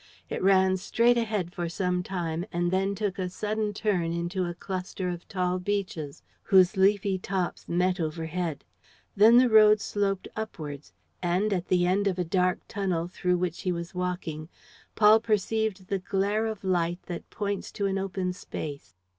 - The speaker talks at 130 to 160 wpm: No, average, 170 wpm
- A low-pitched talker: No, medium, 185 Hz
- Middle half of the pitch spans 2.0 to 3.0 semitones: Yes, narrow, 2.4 semitones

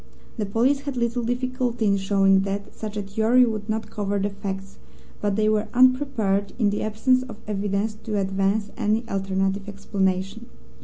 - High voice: Yes, high, 210 Hz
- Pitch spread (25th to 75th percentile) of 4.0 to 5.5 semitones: No, average, 2.9 semitones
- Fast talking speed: No, average, 165 wpm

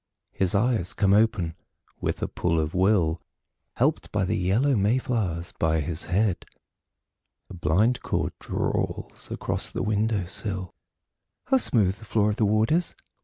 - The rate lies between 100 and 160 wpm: Yes, average, 155 wpm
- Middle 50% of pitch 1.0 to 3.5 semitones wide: No, average, 3.9 semitones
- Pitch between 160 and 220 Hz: No, low, 100 Hz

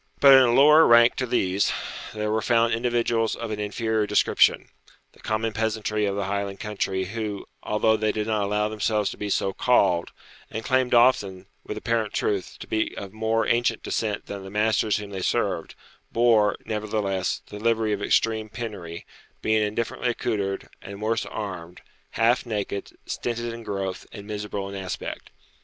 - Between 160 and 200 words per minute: Yes, average, 170 wpm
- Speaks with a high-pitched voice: No, low, 110 Hz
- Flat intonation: Yes, narrow, 2.2 semitones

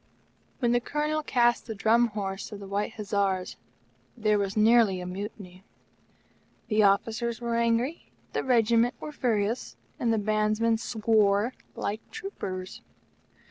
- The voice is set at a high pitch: Yes, high, 220 Hz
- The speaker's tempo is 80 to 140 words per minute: Yes, slow, 135 wpm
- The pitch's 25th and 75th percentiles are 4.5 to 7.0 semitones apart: No, average, 2.7 semitones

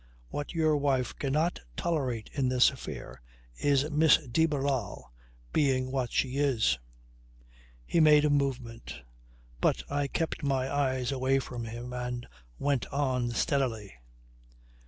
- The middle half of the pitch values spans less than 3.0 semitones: Yes, narrow, 2.6 semitones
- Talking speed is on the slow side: Yes, slow, 130 wpm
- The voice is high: No, low, 135 Hz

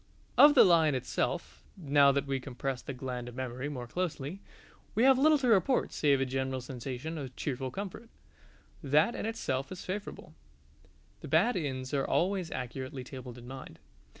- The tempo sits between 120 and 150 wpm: No, average, 170 wpm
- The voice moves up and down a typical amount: No, wide, 5.9 semitones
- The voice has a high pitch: No, medium, 140 Hz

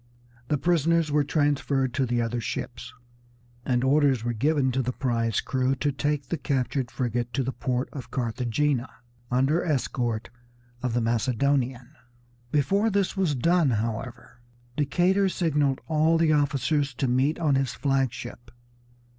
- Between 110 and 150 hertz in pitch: Yes, low, 135 Hz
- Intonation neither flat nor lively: Yes, average, 3.4 semitones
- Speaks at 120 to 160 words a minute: Yes, average, 145 wpm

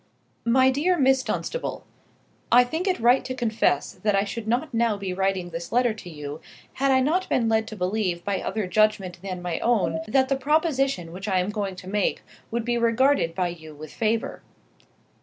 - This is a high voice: Yes, high, 220 Hz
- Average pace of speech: Yes, average, 195 wpm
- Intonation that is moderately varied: No, wide, 5.8 semitones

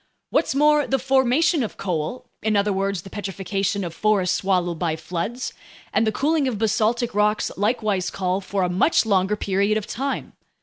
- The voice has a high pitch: Yes, high, 205 Hz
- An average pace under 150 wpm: No, average, 165 wpm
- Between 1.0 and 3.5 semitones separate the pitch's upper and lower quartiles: No, average, 4.1 semitones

